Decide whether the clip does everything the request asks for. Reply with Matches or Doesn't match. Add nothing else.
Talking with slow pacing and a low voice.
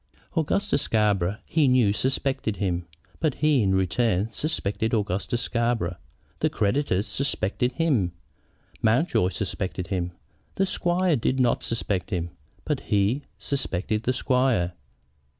Matches